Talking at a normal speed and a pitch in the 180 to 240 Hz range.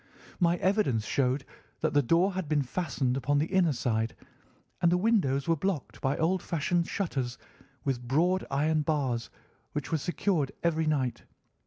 No: average, 160 wpm; medium, 150 Hz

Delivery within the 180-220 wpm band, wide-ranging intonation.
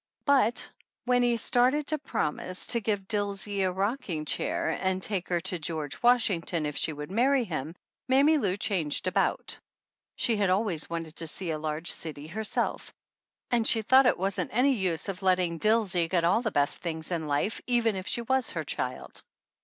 Yes: average, 185 wpm; wide, 5.8 semitones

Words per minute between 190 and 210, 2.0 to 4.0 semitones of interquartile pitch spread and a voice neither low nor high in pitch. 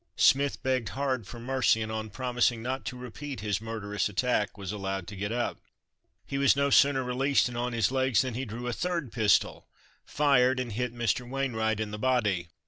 No: average, 200 wpm; average, 3.3 semitones; low, 120 Hz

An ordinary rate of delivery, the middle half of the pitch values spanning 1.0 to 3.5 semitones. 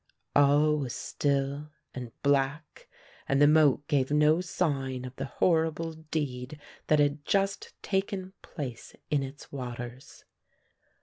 No: slow, 125 wpm; narrow, 2.6 semitones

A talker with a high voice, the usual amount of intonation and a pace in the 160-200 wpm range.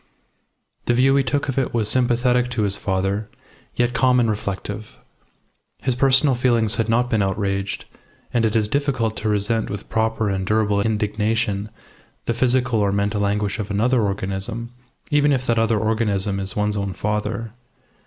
No: low, 110 Hz; average, 3.1 semitones; average, 165 wpm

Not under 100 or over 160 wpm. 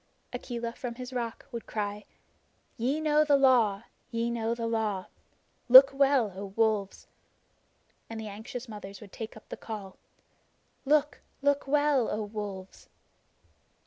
Yes: average, 140 wpm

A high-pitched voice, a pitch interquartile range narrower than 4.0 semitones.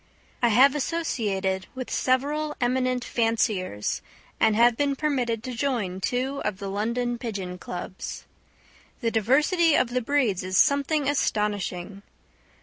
No: high, 240 Hz; average, 5.0 semitones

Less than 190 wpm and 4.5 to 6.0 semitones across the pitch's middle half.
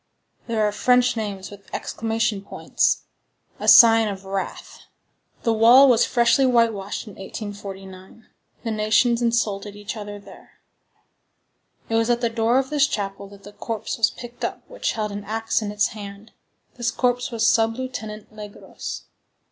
No: average, 155 wpm; narrow, 2.4 semitones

